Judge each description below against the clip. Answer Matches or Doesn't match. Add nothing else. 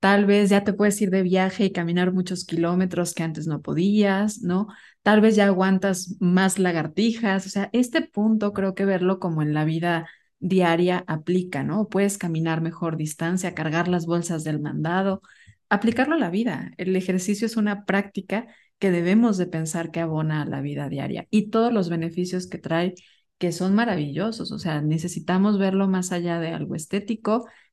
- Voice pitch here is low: Doesn't match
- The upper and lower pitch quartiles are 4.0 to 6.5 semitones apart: Doesn't match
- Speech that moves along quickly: Doesn't match